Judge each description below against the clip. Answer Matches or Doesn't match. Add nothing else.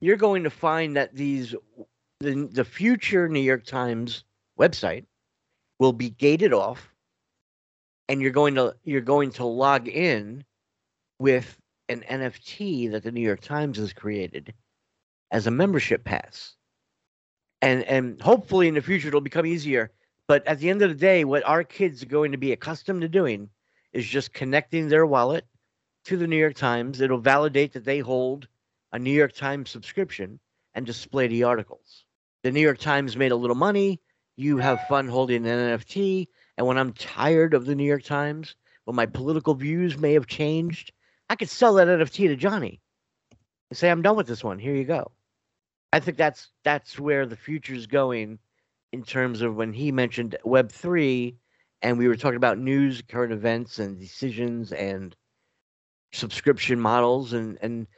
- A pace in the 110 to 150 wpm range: Doesn't match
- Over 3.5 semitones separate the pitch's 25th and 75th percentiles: Matches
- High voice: Doesn't match